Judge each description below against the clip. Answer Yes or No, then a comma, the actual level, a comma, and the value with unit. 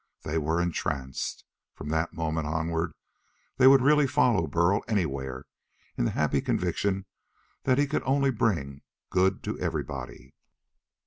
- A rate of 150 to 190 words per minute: No, slow, 135 wpm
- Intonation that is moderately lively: No, wide, 7.6 semitones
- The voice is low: Yes, very low, 85 Hz